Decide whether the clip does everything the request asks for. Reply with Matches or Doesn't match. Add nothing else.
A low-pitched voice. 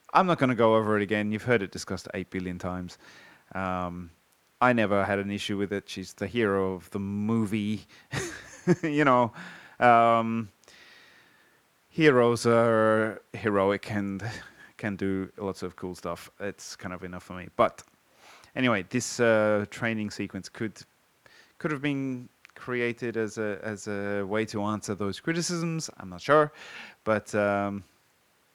Matches